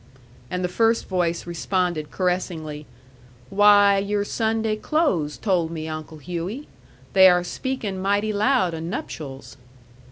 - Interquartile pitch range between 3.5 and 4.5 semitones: Yes, average, 3.9 semitones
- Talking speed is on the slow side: Yes, slow, 125 wpm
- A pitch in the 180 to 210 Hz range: Yes, medium, 185 Hz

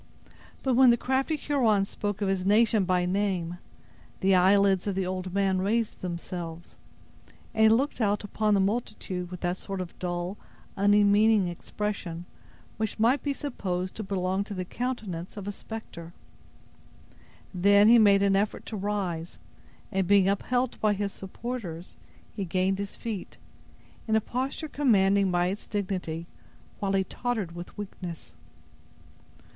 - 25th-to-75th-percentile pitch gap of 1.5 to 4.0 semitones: Yes, average, 3.0 semitones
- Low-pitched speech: No, high, 200 Hz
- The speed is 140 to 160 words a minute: Yes, average, 150 wpm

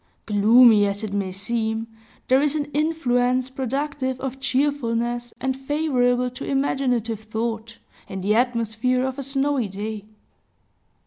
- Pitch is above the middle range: Yes, high, 245 Hz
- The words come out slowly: Yes, slow, 130 wpm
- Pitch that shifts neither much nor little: Yes, average, 3.3 semitones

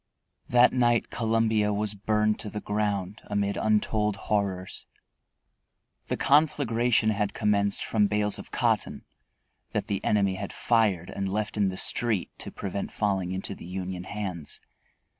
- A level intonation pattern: Yes, narrow, 1.8 semitones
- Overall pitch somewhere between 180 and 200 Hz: No, low, 105 Hz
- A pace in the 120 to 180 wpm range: Yes, average, 140 wpm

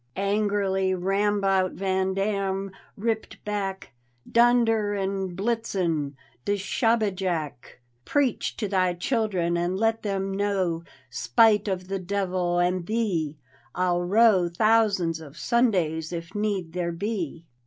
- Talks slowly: Yes, slow, 115 wpm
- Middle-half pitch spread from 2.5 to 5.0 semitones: Yes, average, 2.8 semitones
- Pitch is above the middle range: Yes, high, 195 Hz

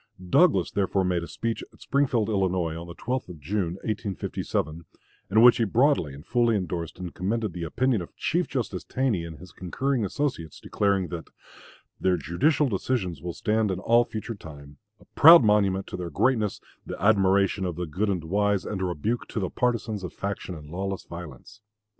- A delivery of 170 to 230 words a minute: Yes, average, 185 wpm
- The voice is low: Yes, very low, 95 Hz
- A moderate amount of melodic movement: Yes, average, 4.7 semitones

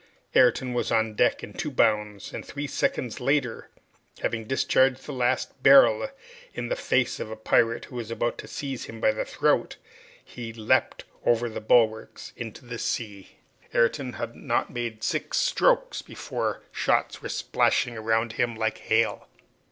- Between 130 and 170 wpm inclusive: Yes, average, 160 wpm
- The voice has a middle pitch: No, low, 115 Hz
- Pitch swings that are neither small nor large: No, narrow, 2.3 semitones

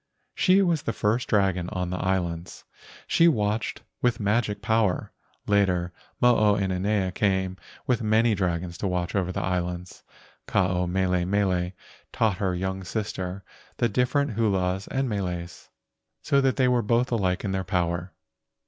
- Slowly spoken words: No, average, 155 wpm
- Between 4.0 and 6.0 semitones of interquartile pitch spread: No, average, 3.4 semitones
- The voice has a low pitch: Yes, very low, 95 Hz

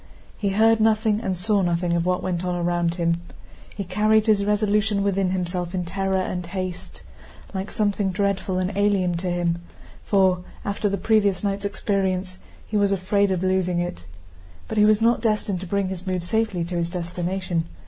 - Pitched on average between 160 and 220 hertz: Yes, high, 190 Hz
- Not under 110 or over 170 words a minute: No, average, 180 wpm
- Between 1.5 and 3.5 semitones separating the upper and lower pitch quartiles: Yes, narrow, 2.4 semitones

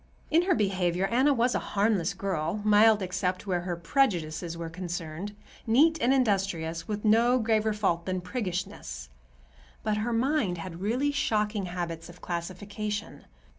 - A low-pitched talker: No, high, 200 Hz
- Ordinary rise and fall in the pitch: Yes, average, 4.3 semitones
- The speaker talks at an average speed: Yes, average, 145 wpm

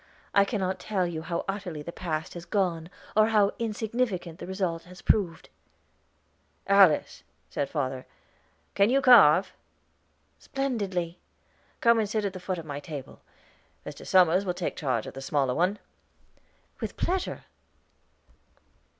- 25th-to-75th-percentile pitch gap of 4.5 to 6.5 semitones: No, average, 4.1 semitones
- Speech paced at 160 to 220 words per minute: No, average, 140 wpm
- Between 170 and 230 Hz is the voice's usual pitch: Yes, medium, 185 Hz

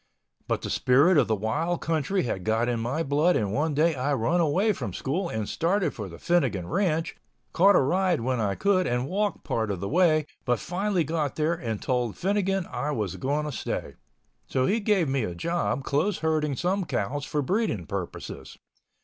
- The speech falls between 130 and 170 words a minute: No, average, 200 wpm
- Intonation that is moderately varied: No, wide, 6.6 semitones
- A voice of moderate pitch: Yes, medium, 150 Hz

